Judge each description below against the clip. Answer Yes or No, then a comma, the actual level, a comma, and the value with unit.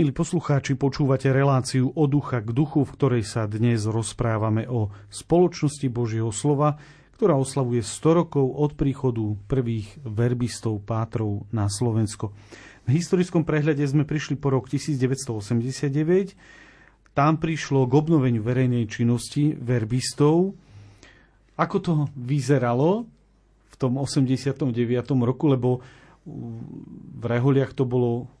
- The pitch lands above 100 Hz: Yes, low, 130 Hz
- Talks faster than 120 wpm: No, average, 115 wpm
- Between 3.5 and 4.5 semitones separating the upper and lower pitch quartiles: Yes, average, 3.9 semitones